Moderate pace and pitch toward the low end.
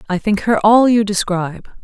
No: average, 195 wpm; high, 205 Hz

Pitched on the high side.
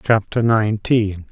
No: low, 110 Hz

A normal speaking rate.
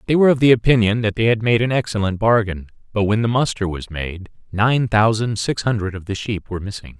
No: fast, 230 wpm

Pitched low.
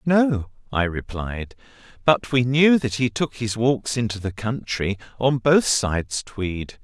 Yes: low, 120 Hz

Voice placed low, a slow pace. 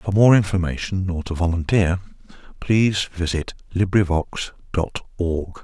Yes: very low, 90 Hz; slow, 115 wpm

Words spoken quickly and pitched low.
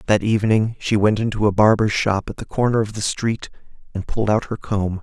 Yes: fast, 225 wpm; low, 105 Hz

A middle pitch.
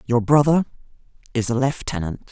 No: low, 125 Hz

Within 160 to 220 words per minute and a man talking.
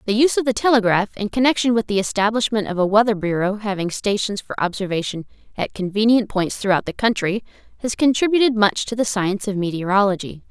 No: average, 185 wpm; female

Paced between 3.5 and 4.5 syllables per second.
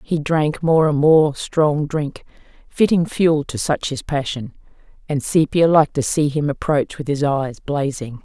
Yes: 4.2 syllables/s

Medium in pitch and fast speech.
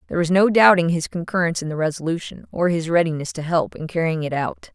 Yes: medium, 165 Hz; fast, 230 wpm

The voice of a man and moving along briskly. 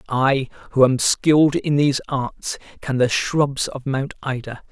No: male; average, 165 wpm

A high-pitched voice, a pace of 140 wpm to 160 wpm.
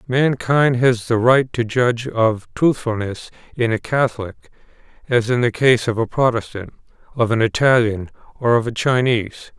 No: low, 120 Hz; average, 155 wpm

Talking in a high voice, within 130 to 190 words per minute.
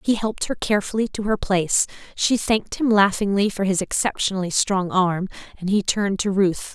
Yes: high, 200 Hz; average, 185 wpm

